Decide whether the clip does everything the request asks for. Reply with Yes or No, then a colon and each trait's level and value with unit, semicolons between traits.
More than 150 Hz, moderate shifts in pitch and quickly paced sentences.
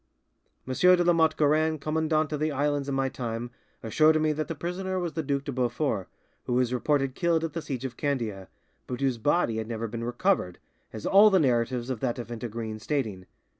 No: medium, 140 Hz; average, 4.7 semitones; fast, 210 wpm